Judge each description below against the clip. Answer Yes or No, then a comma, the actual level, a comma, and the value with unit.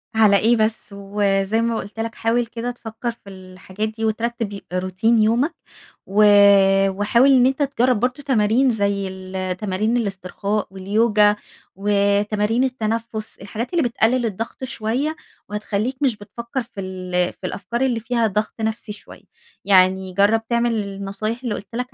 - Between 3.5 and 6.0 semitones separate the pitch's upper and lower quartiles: No, average, 2.9 semitones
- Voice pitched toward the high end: Yes, high, 215 Hz